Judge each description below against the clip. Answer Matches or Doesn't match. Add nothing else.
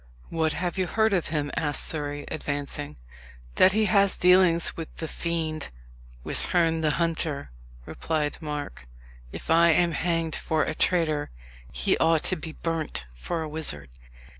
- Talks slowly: Doesn't match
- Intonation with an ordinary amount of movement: Doesn't match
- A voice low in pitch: Doesn't match